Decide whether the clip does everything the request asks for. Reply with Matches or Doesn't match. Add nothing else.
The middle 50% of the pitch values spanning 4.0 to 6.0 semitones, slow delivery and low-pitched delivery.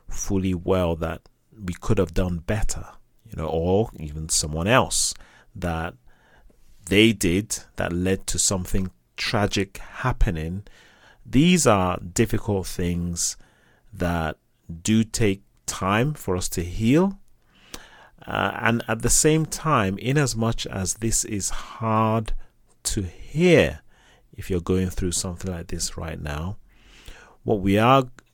Matches